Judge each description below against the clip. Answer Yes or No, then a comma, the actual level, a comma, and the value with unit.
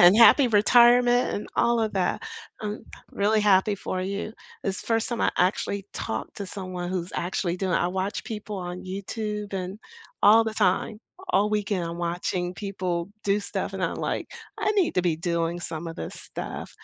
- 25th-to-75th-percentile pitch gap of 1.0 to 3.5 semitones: Yes, average, 2.9 semitones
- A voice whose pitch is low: No, high, 195 Hz